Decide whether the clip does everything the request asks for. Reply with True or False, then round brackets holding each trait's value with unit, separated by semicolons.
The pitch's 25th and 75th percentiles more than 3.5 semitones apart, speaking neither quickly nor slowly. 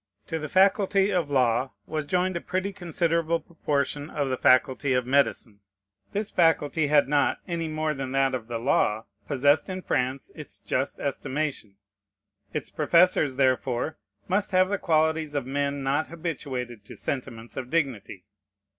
True (4.2 semitones; 155 wpm)